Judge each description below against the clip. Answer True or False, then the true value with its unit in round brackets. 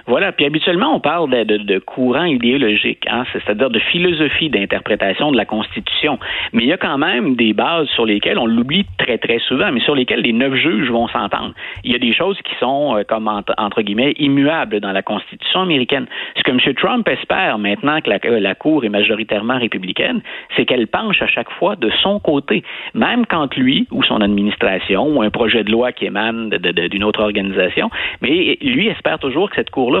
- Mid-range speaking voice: False (115 Hz)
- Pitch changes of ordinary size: False (7.7 semitones)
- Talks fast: False (210 wpm)